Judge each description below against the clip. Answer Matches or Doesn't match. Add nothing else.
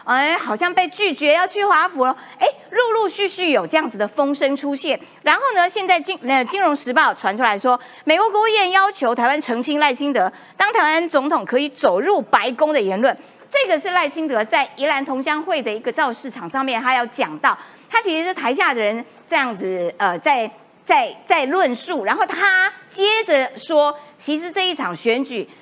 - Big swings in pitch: Matches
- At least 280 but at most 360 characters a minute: Matches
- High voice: Matches